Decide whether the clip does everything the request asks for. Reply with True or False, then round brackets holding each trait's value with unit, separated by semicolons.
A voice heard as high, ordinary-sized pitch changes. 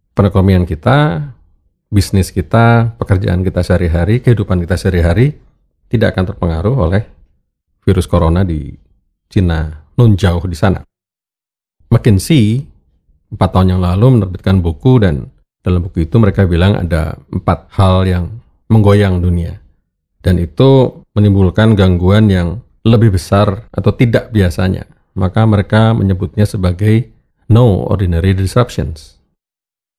False (95 Hz; 3.9 semitones)